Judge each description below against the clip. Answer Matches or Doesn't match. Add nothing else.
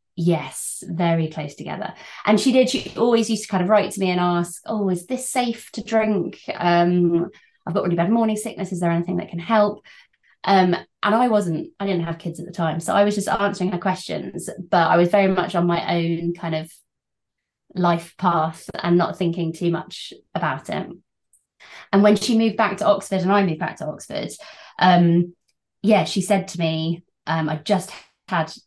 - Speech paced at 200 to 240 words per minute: Matches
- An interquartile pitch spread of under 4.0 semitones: Matches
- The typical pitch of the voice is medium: Matches